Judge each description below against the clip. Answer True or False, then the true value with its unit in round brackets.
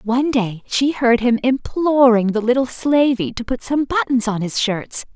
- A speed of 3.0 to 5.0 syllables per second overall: True (4.5 syllables/s)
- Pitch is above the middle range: True (245 Hz)